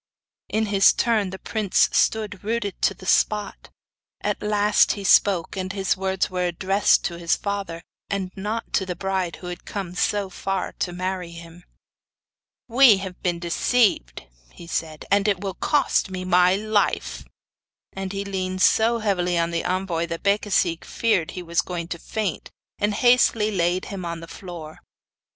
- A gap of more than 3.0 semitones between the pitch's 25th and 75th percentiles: No, narrow, 2.5 semitones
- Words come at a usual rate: Yes, average, 170 wpm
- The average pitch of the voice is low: No, high, 190 Hz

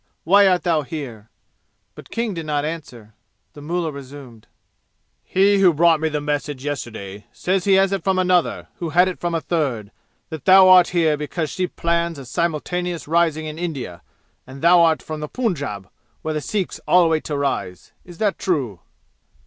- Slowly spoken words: No, average, 180 wpm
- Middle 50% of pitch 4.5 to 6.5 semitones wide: No, average, 3.9 semitones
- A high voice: No, medium, 160 Hz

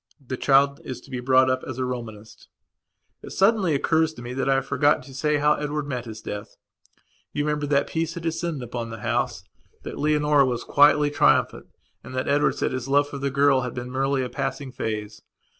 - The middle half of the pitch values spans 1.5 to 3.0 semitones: Yes, average, 2.7 semitones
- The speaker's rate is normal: No, fast, 210 wpm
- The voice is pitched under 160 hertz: Yes, low, 135 Hz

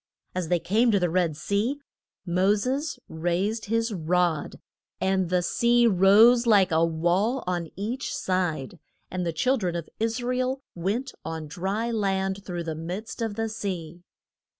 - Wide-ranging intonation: No, average, 4.7 semitones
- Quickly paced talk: No, average, 170 wpm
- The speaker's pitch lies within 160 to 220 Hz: Yes, high, 190 Hz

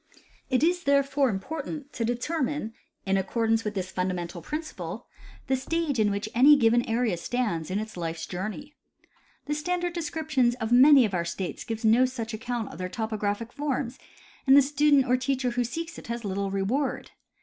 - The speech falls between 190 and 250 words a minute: No, average, 175 wpm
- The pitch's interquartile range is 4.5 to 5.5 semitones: Yes, average, 5.2 semitones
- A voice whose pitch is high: Yes, high, 245 Hz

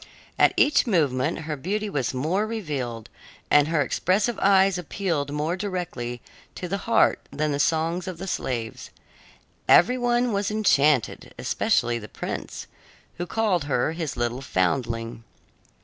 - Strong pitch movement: Yes, wide, 7.0 semitones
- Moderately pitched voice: Yes, medium, 160 Hz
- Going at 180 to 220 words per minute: No, average, 140 wpm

